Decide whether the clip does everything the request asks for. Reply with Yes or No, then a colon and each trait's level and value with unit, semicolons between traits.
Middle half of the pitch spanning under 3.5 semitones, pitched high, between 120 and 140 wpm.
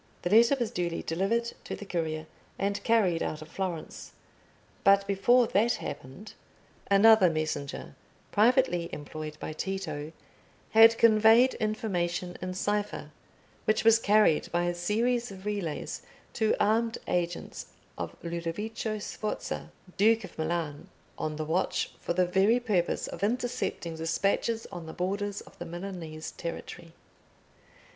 No: average, 4.5 semitones; high, 195 Hz; slow, 135 wpm